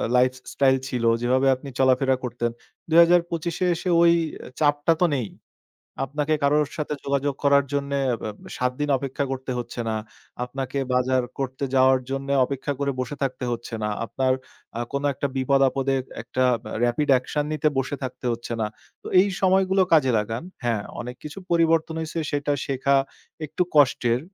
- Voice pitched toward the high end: No, low, 135 Hz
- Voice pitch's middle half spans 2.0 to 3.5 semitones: Yes, narrow, 2.5 semitones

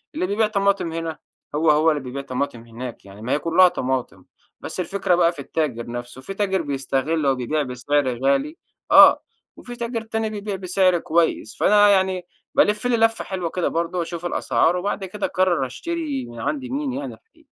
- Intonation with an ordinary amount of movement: No, wide, 6.8 semitones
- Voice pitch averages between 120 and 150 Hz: No, medium, 175 Hz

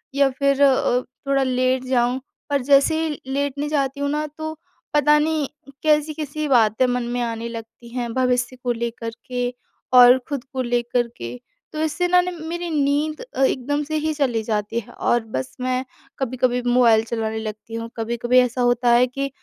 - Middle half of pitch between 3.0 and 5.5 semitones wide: Yes, average, 3.3 semitones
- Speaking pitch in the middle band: No, very high, 255 Hz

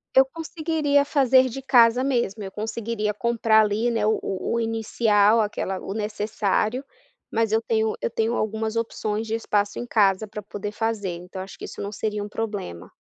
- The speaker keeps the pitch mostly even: Yes, narrow, 2.1 semitones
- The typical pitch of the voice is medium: No, high, 220 Hz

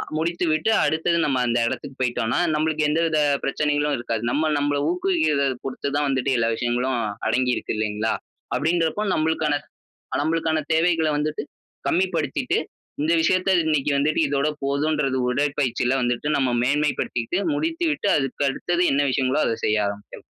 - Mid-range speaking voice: Yes, medium, 145 Hz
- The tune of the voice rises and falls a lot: No, average, 3.6 semitones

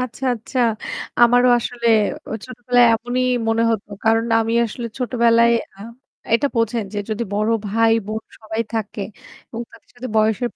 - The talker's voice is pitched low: No, high, 230 Hz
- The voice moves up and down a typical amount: No, narrow, 1.6 semitones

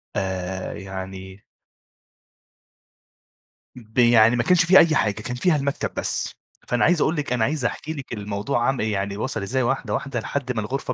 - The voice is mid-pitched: No, low, 120 Hz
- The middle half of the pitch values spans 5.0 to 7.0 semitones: Yes, average, 5.3 semitones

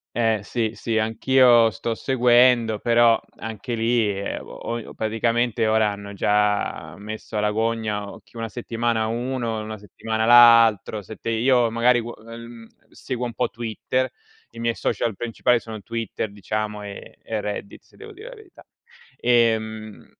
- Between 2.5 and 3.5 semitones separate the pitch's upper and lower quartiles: No, narrow, 1.6 semitones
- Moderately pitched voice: No, low, 115 Hz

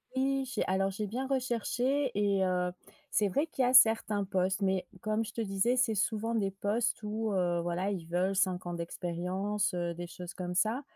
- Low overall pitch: No, high, 200 Hz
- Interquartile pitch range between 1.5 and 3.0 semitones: No, average, 3.9 semitones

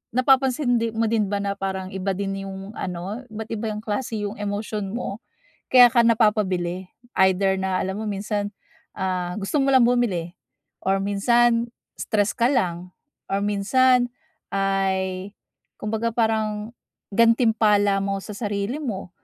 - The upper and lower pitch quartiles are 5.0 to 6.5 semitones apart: No, average, 3.0 semitones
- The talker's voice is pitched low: No, high, 205 Hz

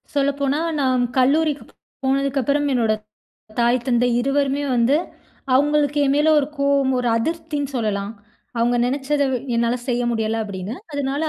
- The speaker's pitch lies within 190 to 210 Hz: No, very high, 270 Hz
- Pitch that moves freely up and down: No, average, 3.0 semitones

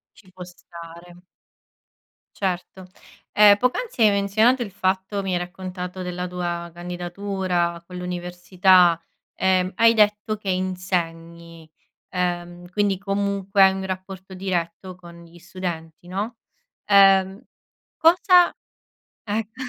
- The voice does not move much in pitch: Yes, narrow, 2.2 semitones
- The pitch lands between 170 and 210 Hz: Yes, medium, 185 Hz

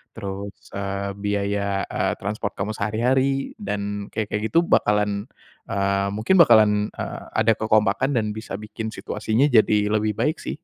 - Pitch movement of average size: No, narrow, 1.6 semitones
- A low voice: Yes, low, 105 Hz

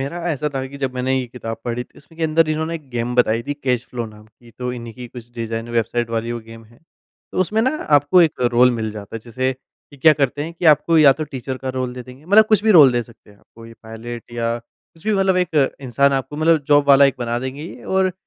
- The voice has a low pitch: Yes, low, 130 Hz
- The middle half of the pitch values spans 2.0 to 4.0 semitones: No, average, 4.4 semitones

